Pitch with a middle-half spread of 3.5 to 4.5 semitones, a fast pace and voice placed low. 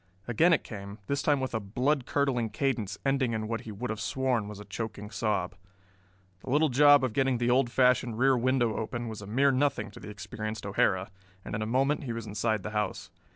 Yes: average, 3.8 semitones; fast, 220 wpm; low, 115 Hz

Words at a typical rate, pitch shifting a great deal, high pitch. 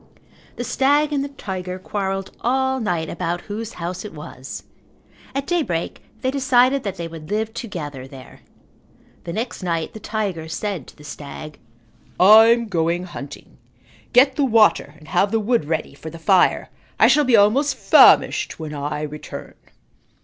Yes: average, 160 wpm; wide, 6.7 semitones; high, 195 Hz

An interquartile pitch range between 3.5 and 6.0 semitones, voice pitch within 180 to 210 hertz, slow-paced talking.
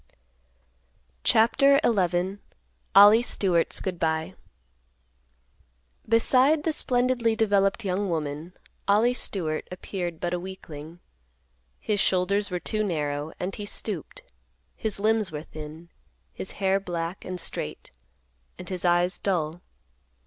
Yes: average, 3.8 semitones; high, 190 Hz; slow, 115 wpm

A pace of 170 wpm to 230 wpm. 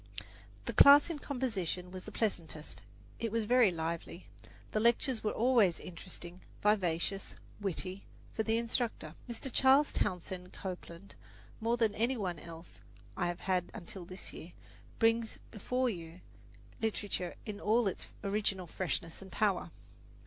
No: average, 140 wpm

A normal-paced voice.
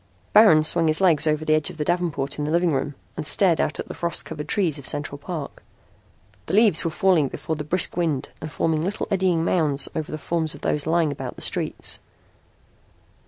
No: fast, 210 wpm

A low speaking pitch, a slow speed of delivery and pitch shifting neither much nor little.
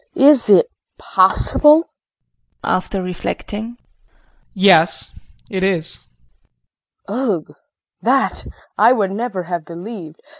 No: high, 195 Hz; slow, 100 wpm; average, 5.0 semitones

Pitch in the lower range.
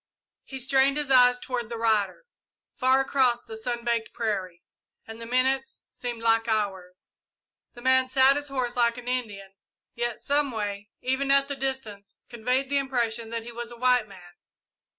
No: high, 240 Hz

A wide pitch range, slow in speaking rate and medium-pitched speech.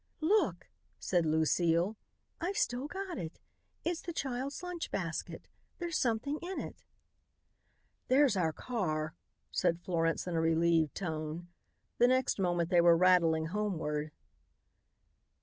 Yes: wide, 8.4 semitones; slow, 125 wpm; medium, 180 Hz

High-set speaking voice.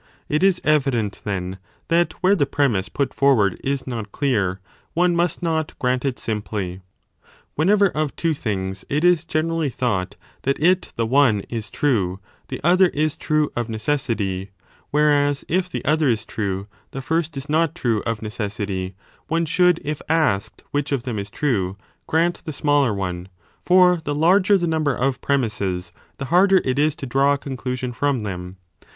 No: medium, 140 Hz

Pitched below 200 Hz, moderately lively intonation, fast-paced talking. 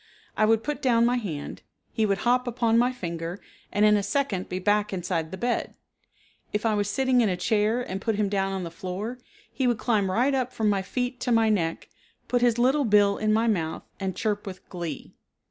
No: high, 215 Hz; average, 4.0 semitones; fast, 220 wpm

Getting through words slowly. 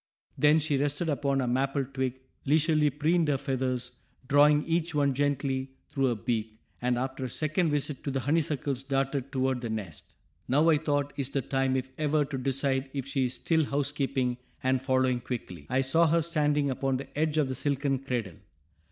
No: average, 185 wpm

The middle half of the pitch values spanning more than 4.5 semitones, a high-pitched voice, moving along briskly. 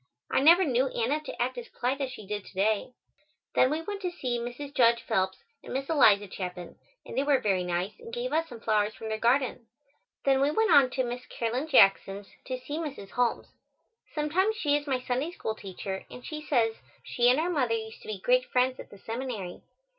Yes: average, 4.9 semitones; very high, 250 Hz; fast, 215 wpm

